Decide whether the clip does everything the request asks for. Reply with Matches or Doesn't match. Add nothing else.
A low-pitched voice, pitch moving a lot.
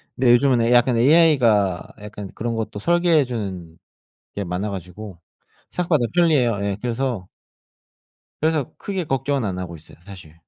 Matches